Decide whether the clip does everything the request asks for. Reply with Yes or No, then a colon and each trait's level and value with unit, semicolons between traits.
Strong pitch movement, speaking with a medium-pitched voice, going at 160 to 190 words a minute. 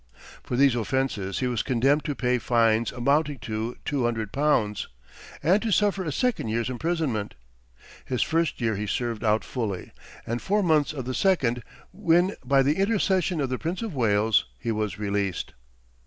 No: wide, 5.9 semitones; low, 125 Hz; average, 170 wpm